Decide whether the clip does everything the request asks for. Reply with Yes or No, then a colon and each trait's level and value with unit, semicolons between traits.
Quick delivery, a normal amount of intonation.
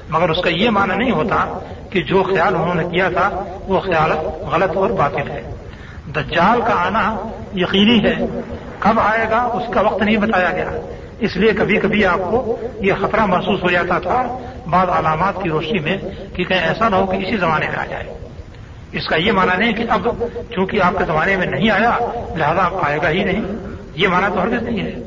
Yes: fast, 205 wpm; average, 3.6 semitones